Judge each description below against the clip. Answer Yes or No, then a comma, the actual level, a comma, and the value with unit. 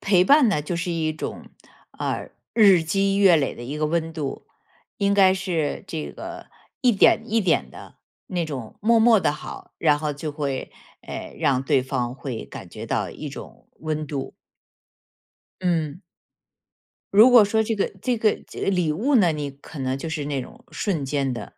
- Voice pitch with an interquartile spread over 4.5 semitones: Yes, wide, 5.5 semitones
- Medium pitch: Yes, medium, 165 Hz